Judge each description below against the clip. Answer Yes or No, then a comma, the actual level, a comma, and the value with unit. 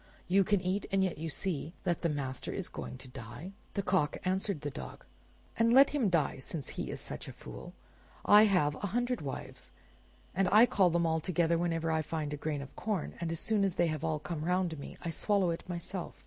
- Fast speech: Yes, fast, 220 wpm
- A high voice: No, medium, 170 Hz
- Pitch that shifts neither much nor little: Yes, average, 4.1 semitones